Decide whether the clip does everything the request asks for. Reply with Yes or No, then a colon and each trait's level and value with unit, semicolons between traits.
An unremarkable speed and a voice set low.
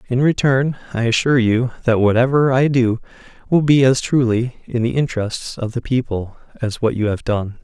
Yes: average, 190 wpm; low, 125 Hz